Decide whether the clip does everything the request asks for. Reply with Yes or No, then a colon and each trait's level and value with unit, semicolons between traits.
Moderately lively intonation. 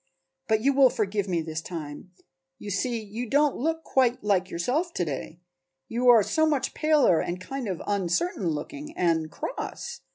No: wide, 7.5 semitones